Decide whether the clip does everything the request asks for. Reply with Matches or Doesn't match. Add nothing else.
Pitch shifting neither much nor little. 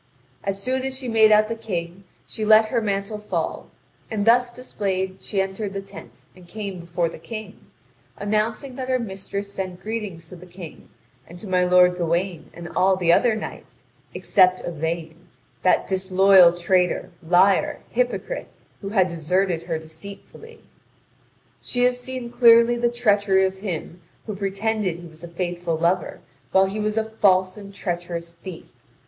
Matches